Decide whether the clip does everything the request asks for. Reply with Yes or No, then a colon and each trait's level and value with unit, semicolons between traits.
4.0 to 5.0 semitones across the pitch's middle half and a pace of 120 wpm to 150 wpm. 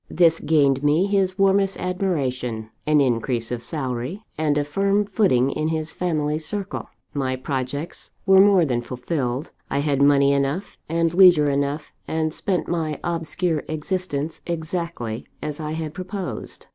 Yes: average, 4.4 semitones; average, 145 wpm